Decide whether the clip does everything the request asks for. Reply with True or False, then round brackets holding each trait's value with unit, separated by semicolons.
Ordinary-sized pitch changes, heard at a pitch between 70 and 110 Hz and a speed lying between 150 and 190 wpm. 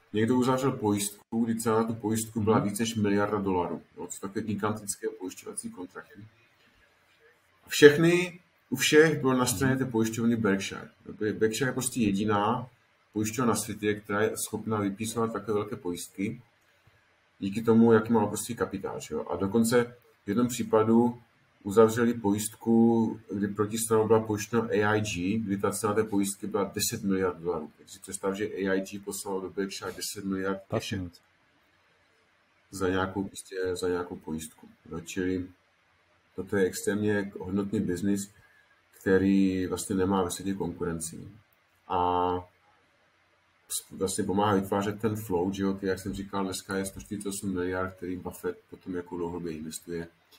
False (3.0 semitones; 105 Hz; 135 wpm)